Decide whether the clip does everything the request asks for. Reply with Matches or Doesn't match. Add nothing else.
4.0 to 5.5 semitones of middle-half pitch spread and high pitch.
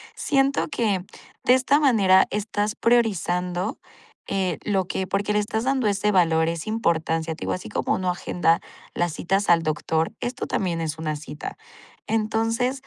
Matches